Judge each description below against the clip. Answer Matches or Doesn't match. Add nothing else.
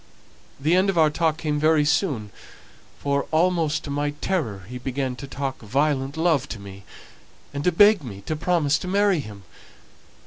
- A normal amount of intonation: Matches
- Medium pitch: Matches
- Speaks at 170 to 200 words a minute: Matches